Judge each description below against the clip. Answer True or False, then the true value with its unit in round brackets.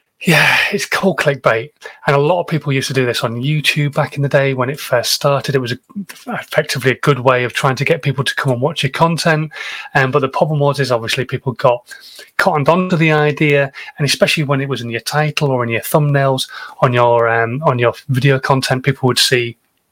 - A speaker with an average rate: False (225 wpm)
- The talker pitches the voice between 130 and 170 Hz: True (140 Hz)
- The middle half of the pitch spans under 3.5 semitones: True (2.9 semitones)